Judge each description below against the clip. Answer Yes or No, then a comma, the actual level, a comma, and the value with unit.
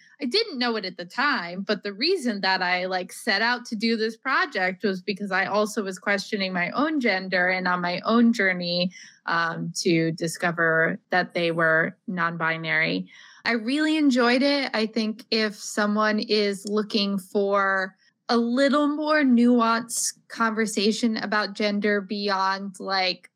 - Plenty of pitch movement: No, average, 3.9 semitones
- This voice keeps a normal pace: Yes, average, 155 wpm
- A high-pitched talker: Yes, high, 205 Hz